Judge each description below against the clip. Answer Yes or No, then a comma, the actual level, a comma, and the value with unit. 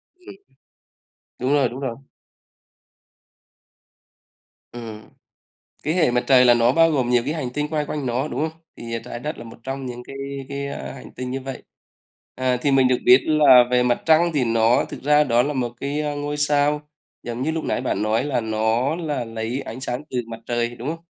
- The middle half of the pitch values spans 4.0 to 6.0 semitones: No, average, 3.5 semitones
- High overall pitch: No, low, 130 Hz